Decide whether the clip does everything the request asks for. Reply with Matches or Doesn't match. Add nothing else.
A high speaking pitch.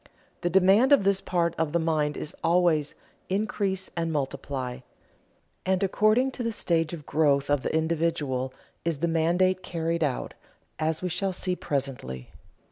Doesn't match